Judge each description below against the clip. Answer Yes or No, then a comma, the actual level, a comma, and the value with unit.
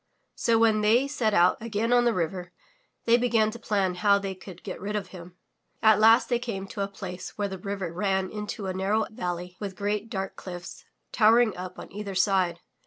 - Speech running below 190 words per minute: No, average, 200 wpm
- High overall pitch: Yes, high, 200 Hz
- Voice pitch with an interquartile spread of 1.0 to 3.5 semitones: Yes, average, 2.8 semitones